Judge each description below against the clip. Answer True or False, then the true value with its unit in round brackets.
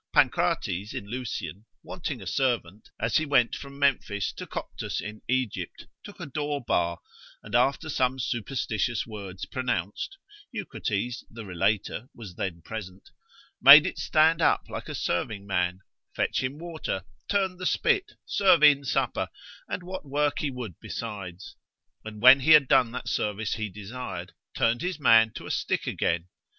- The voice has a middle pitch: False (120 Hz)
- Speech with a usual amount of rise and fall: False (6.0 semitones)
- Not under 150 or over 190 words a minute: True (160 wpm)